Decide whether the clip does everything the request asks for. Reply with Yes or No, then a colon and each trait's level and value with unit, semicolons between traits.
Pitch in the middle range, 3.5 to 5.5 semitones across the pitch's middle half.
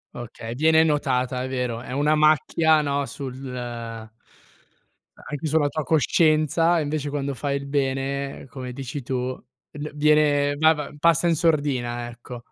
No: medium, 145 Hz; average, 2.7 semitones